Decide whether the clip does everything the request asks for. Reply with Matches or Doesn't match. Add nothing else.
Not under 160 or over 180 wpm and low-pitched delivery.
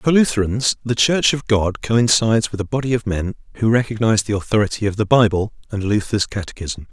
Doesn't match